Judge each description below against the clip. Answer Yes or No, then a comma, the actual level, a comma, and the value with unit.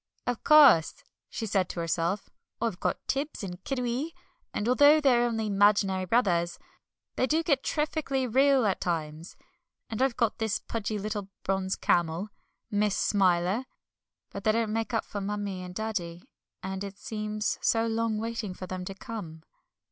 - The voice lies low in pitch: No, high, 210 Hz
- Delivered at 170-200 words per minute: No, average, 160 wpm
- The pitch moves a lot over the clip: No, average, 4.0 semitones